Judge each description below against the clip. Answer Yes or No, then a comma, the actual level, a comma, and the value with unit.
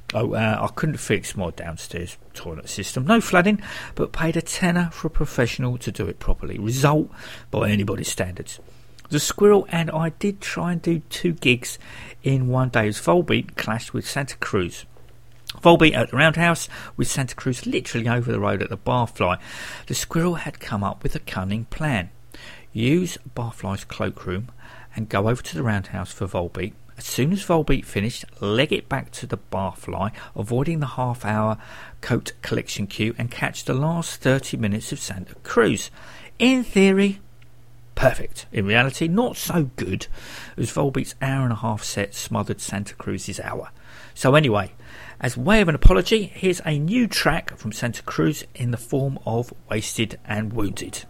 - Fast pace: No, average, 170 wpm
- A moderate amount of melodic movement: No, wide, 6.5 semitones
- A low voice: Yes, low, 125 Hz